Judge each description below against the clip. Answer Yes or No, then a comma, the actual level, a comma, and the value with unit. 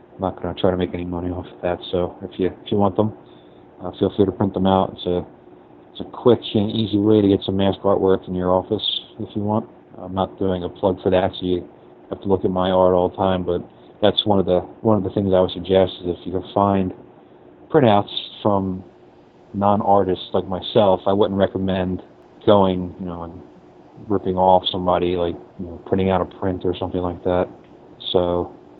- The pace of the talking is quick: Yes, fast, 225 wpm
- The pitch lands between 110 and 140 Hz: No, very low, 95 Hz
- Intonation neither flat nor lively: No, narrow, 1.7 semitones